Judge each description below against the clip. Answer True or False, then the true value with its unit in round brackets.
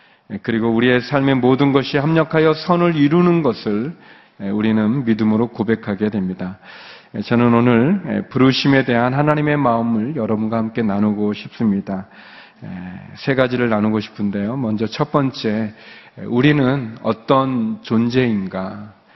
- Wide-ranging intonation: False (4.5 semitones)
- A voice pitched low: True (115 Hz)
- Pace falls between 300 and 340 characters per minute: False (290 characters per minute)